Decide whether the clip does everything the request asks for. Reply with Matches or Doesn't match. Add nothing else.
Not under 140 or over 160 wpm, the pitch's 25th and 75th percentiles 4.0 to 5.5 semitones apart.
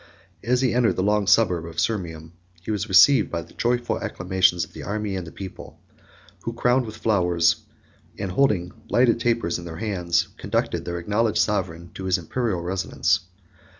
Doesn't match